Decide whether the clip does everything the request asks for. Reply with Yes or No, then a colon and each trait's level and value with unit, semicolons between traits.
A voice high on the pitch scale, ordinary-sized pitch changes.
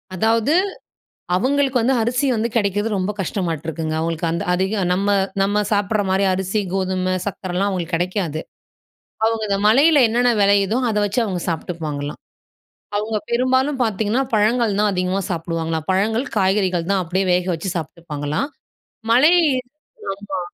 Yes: high, 195 Hz; average, 3.8 semitones